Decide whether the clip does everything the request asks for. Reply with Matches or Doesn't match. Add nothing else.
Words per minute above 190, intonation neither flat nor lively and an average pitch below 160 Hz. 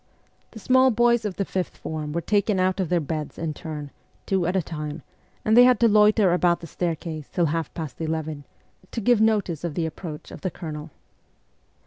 Doesn't match